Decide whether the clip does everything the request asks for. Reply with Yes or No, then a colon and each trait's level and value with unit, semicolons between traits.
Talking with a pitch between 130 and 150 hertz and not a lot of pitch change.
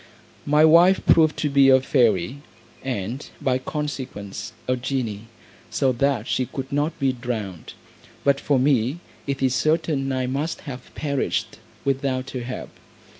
Yes: low, 135 Hz; narrow, 2.3 semitones